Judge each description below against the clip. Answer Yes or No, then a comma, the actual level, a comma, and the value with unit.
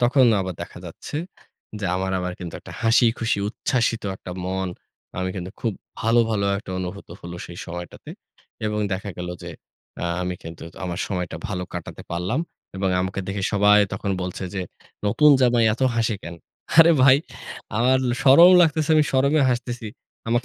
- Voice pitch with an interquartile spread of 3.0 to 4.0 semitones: No, average, 5.0 semitones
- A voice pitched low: Yes, low, 105 Hz